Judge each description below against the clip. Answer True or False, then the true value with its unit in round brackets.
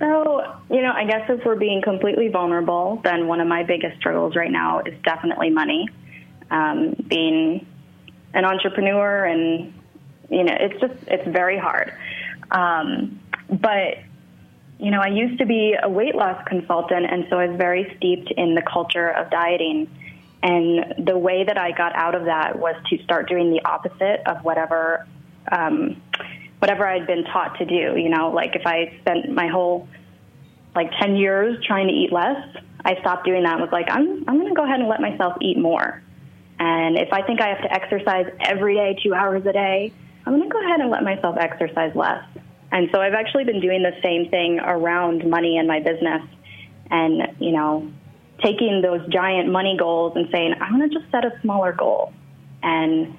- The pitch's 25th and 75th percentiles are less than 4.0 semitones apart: True (3.4 semitones)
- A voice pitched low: False (180 Hz)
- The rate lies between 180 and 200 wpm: True (190 wpm)